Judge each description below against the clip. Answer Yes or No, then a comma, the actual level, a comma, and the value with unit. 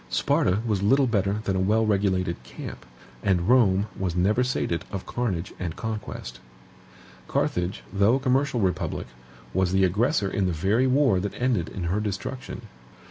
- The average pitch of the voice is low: Yes, low, 100 Hz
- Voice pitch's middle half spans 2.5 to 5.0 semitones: Yes, average, 4.2 semitones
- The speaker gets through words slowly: No, average, 155 wpm